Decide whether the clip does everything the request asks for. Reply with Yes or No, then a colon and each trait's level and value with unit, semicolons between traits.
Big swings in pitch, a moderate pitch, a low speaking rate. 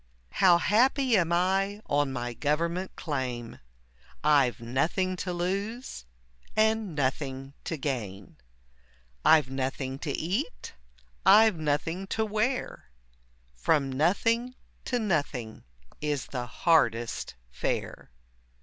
Yes: wide, 6.8 semitones; medium, 160 Hz; slow, 105 wpm